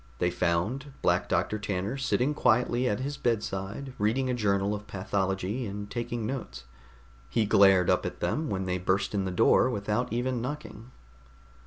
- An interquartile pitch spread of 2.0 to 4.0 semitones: No, average, 4.4 semitones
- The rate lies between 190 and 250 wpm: No, average, 165 wpm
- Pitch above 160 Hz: No, low, 105 Hz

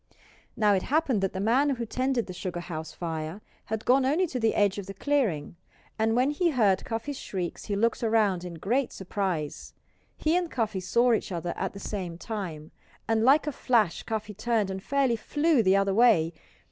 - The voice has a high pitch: Yes, high, 215 Hz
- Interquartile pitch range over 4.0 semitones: Yes, average, 5.1 semitones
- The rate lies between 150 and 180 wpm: No, average, 195 wpm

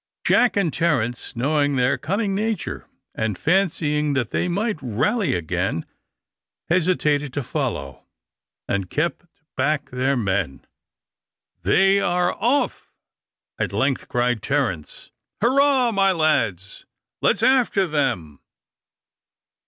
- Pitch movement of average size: No, wide, 8.5 semitones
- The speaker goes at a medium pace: No, slow, 105 wpm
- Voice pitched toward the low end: No, medium, 150 Hz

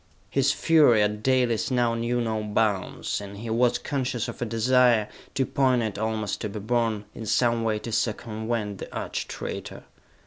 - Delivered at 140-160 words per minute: No, average, 170 wpm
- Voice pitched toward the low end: Yes, low, 115 Hz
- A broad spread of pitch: No, narrow, 2.4 semitones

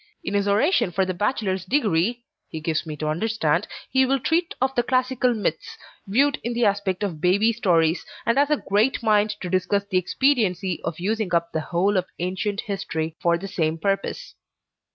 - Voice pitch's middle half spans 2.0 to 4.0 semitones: No, average, 4.9 semitones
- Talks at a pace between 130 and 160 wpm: No, average, 190 wpm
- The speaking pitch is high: Yes, high, 200 Hz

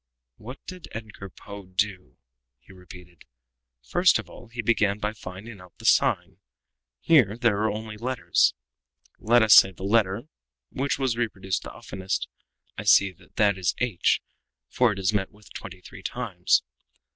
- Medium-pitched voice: No, low, 105 Hz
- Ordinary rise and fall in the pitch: Yes, average, 3.5 semitones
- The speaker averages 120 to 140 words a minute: No, average, 160 wpm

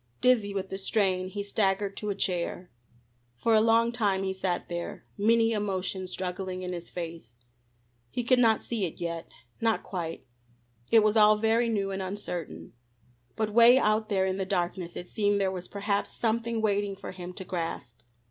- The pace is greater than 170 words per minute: Yes, average, 180 wpm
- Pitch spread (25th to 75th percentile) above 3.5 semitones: No, average, 3.0 semitones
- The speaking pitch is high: Yes, high, 200 Hz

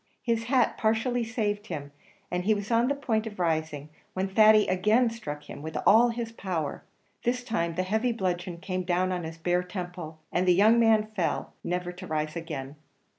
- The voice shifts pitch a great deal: No, average, 4.5 semitones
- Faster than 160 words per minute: Yes, average, 190 wpm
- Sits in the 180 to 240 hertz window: Yes, medium, 185 Hz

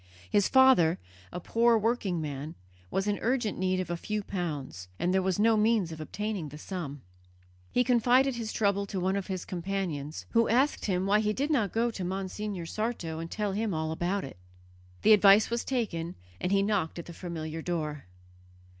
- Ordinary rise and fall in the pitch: Yes, average, 4.4 semitones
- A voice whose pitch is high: Yes, high, 195 Hz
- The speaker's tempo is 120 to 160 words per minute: No, average, 190 wpm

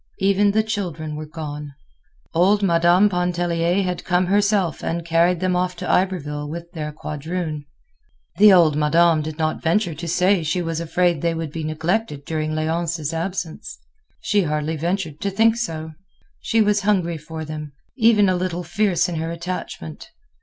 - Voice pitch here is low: No, medium, 170 Hz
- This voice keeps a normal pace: Yes, average, 160 wpm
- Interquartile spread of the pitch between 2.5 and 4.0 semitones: Yes, average, 2.9 semitones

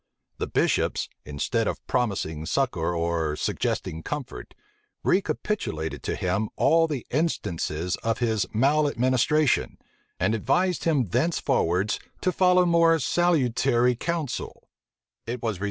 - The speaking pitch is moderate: No, low, 125 Hz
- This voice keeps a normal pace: No, slow, 105 wpm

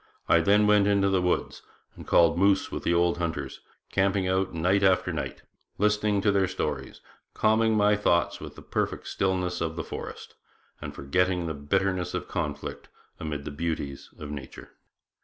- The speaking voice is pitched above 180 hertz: No, very low, 90 Hz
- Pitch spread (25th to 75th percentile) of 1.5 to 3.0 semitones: No, average, 3.5 semitones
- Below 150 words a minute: No, average, 170 wpm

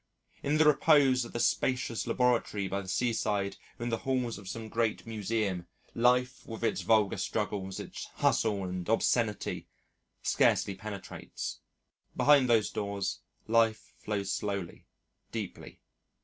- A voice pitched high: No, low, 110 Hz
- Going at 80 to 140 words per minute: Yes, slow, 135 wpm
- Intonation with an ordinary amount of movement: Yes, average, 3.4 semitones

